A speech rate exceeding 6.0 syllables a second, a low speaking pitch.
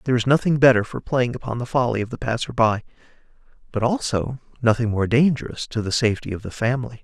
Yes: 6.6 syllables/s; low, 120 Hz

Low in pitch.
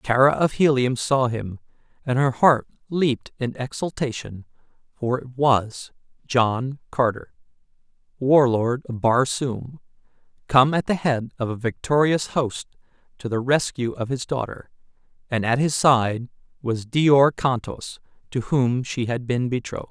Yes: low, 130 Hz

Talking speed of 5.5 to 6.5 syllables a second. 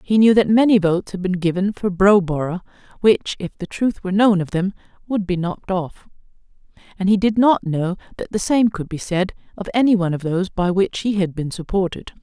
Yes: 5.7 syllables/s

